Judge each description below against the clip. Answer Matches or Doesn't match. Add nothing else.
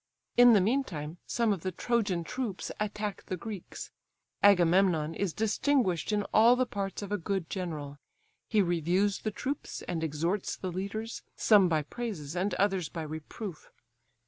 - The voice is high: Matches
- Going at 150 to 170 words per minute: Matches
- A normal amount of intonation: Matches